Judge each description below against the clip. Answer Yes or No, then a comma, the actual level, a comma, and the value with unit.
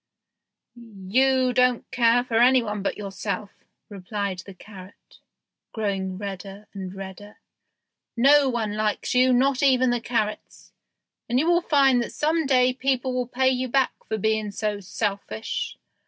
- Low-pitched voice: No, high, 230 Hz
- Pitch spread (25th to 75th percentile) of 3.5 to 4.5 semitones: Yes, average, 4.1 semitones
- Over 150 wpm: No, average, 140 wpm